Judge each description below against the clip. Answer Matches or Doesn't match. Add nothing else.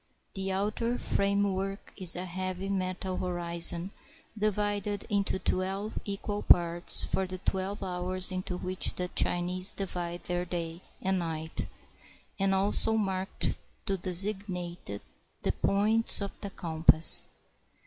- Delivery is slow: Matches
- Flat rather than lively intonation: Matches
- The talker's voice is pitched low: Doesn't match